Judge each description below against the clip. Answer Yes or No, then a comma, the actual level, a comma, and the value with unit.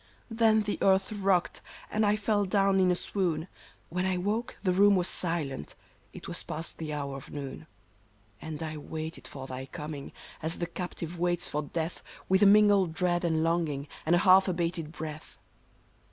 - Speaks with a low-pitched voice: No, medium, 175 Hz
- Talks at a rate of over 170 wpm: Yes, average, 180 wpm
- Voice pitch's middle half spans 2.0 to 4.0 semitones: Yes, average, 3.7 semitones